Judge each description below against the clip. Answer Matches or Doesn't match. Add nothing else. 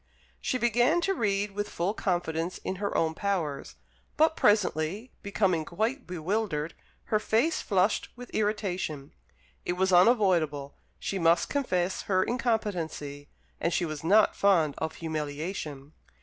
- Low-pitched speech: Doesn't match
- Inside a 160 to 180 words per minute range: Doesn't match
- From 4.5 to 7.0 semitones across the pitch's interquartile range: Matches